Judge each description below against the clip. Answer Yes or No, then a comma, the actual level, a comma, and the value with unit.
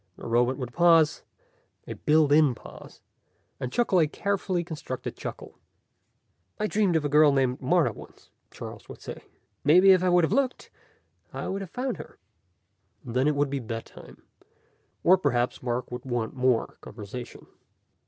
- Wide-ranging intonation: Yes, wide, 6.0 semitones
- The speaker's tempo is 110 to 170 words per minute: Yes, average, 165 wpm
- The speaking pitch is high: No, medium, 145 Hz